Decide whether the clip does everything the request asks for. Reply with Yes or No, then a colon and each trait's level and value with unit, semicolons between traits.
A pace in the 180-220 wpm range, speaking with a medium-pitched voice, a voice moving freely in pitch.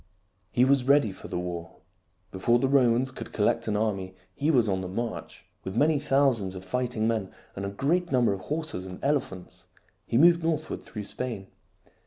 No: average, 190 wpm; low, 115 Hz; wide, 6.3 semitones